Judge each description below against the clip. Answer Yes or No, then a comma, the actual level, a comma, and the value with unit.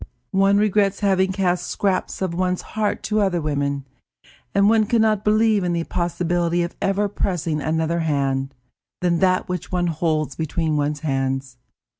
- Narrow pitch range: No, average, 4.1 semitones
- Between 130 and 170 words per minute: Yes, average, 160 wpm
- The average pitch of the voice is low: No, medium, 175 Hz